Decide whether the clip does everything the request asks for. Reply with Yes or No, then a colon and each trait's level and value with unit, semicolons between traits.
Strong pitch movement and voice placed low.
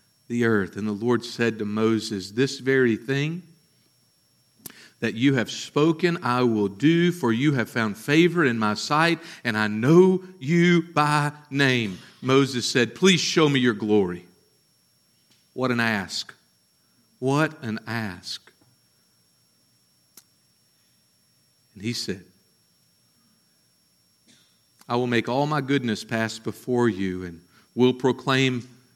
No: average, 4.7 semitones; low, 120 Hz